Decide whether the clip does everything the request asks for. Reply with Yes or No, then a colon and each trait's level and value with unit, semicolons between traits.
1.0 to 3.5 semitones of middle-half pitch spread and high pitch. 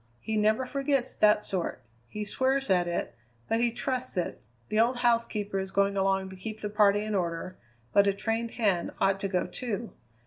Yes: average, 3.2 semitones; high, 210 Hz